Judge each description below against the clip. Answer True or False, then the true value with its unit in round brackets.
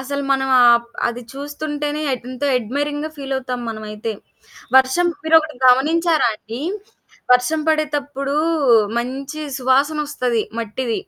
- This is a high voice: True (270 Hz)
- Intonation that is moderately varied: True (3.1 semitones)